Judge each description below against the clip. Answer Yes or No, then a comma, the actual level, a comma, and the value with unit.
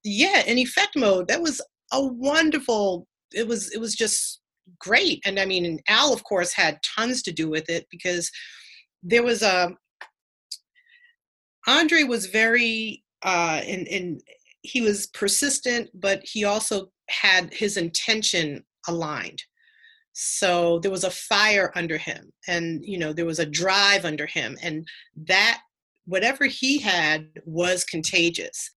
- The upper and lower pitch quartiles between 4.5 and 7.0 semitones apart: Yes, wide, 5.6 semitones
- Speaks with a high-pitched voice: Yes, high, 200 Hz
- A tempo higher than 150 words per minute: No, average, 145 wpm